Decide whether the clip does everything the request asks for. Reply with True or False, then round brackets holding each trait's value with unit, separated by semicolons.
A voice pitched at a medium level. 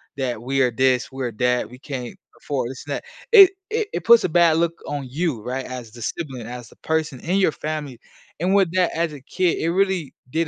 True (145 Hz)